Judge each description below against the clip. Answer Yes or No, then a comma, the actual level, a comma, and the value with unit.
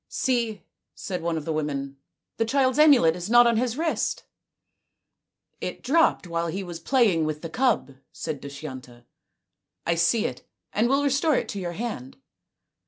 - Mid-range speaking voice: Yes, medium, 180 Hz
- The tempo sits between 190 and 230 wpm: No, average, 180 wpm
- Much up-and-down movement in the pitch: Yes, wide, 7.6 semitones